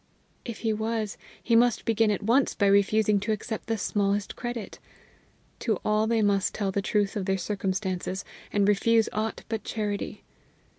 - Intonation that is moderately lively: No, narrow, 1.9 semitones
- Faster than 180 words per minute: No, average, 165 wpm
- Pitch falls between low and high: No, high, 210 Hz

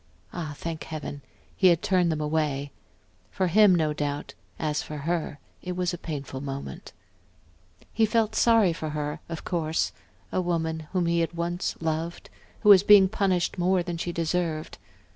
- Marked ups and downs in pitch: No, average, 2.8 semitones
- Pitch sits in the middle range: Yes, medium, 170 Hz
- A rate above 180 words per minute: No, average, 165 wpm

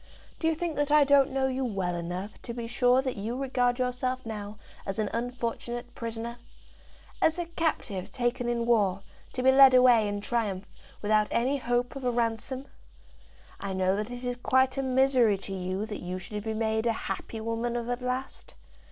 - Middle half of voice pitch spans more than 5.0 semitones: No, average, 3.3 semitones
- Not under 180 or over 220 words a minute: Yes, average, 195 wpm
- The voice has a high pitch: Yes, high, 240 Hz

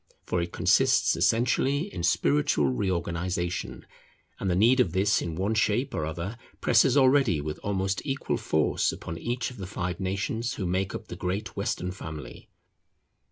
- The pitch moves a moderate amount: Yes, average, 4.7 semitones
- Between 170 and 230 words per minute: No, average, 160 wpm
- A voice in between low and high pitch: No, very low, 95 Hz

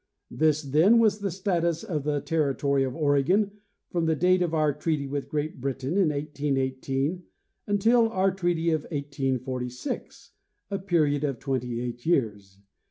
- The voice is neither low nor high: Yes, medium, 150 Hz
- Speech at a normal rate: Yes, average, 150 wpm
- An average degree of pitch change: Yes, average, 4.5 semitones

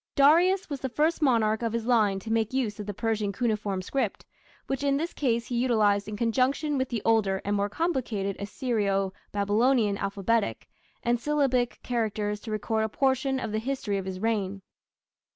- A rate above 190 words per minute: No, average, 180 wpm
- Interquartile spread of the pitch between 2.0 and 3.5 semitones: No, average, 4.2 semitones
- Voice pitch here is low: No, high, 225 Hz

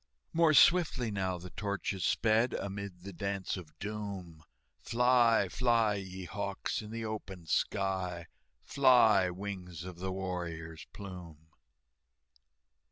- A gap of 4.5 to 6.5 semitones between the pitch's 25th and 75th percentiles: No, average, 3.2 semitones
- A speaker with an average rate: No, slow, 115 wpm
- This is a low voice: Yes, low, 100 Hz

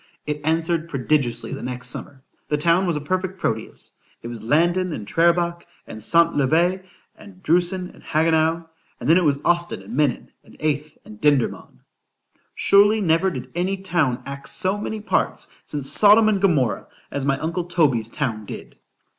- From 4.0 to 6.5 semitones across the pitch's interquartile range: Yes, average, 4.4 semitones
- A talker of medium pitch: Yes, medium, 160 Hz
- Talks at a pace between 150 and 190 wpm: Yes, average, 155 wpm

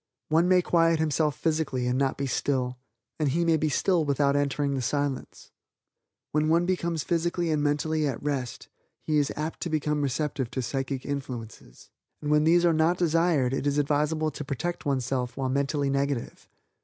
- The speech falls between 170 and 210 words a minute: Yes, average, 180 wpm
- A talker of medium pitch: Yes, medium, 145 Hz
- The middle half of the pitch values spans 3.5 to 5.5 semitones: No, average, 2.7 semitones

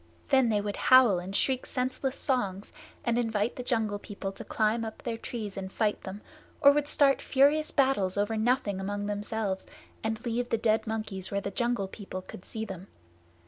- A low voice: No, high, 220 Hz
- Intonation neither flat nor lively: Yes, average, 3.4 semitones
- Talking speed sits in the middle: Yes, average, 185 wpm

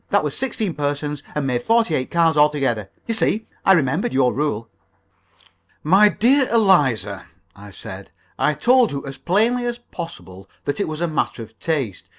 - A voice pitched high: No, medium, 150 Hz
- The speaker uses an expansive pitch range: Yes, wide, 8.1 semitones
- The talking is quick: No, average, 170 wpm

